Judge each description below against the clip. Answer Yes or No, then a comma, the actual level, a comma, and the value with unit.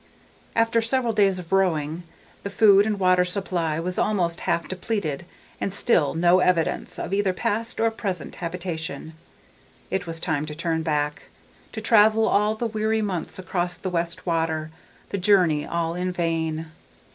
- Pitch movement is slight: No, average, 3.8 semitones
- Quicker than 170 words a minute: No, average, 155 wpm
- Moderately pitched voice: Yes, medium, 180 Hz